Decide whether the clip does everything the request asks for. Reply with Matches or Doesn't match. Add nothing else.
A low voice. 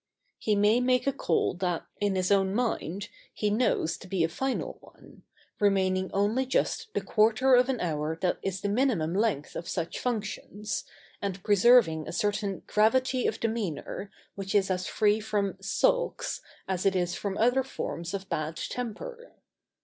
Doesn't match